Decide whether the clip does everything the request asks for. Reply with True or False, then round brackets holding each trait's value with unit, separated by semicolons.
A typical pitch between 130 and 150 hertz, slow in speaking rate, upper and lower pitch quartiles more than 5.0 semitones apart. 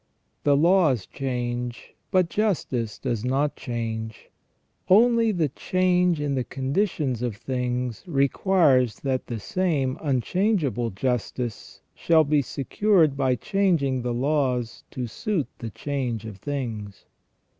True (135 Hz; 120 wpm; 5.4 semitones)